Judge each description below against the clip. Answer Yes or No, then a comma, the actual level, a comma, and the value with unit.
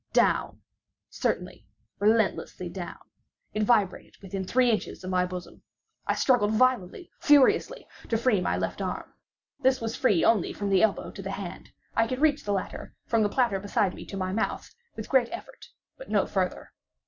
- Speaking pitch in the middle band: No, high, 210 Hz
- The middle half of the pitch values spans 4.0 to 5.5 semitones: Yes, average, 4.5 semitones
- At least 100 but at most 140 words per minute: No, average, 170 wpm